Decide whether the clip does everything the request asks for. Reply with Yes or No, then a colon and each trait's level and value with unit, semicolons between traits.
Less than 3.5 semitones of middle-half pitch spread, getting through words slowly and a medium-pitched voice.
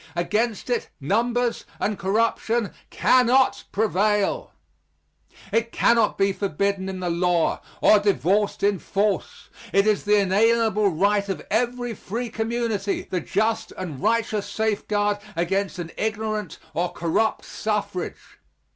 No: narrow, 2.6 semitones; slow, 120 wpm; high, 210 Hz